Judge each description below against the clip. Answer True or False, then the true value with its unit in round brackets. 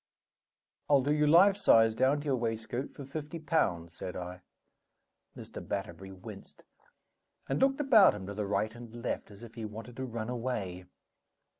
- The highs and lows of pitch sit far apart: True (6.1 semitones)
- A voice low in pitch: True (120 Hz)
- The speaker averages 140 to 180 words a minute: True (170 wpm)